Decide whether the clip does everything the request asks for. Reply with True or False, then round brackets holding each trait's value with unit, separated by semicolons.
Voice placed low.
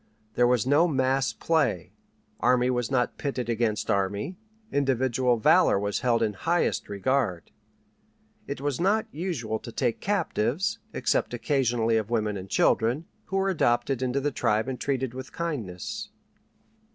True (125 Hz)